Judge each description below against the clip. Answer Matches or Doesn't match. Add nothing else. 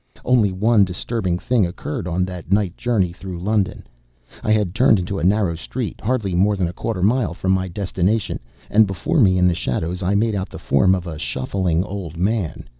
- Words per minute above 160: Matches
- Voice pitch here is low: Matches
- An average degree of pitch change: Matches